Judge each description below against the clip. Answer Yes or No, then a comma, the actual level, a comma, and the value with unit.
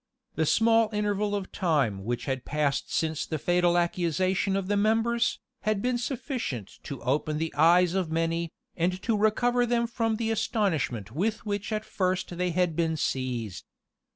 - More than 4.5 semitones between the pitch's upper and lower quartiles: Yes, wide, 5.5 semitones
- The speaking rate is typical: Yes, average, 165 wpm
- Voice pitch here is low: No, medium, 180 Hz